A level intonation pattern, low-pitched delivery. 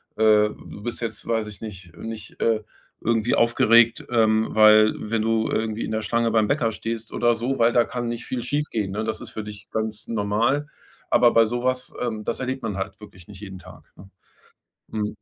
Yes: narrow, 1.7 semitones; low, 110 Hz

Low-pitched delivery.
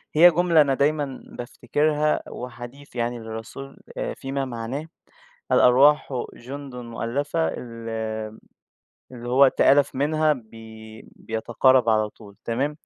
Yes: low, 125 Hz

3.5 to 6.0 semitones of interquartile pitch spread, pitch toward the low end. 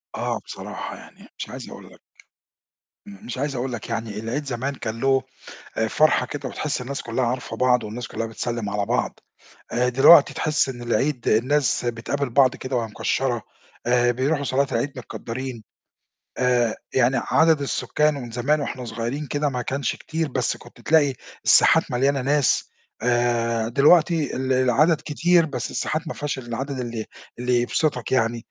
No: average, 3.1 semitones; low, 130 Hz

